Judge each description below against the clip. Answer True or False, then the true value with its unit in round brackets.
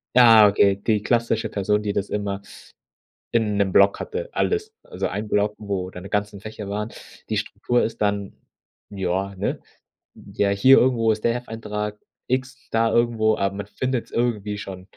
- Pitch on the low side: True (105 Hz)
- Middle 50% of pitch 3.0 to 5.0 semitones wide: False (2.6 semitones)